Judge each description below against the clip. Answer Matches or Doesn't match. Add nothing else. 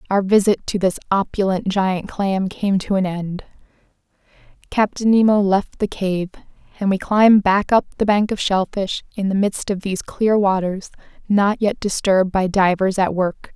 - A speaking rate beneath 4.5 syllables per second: Doesn't match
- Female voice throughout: Matches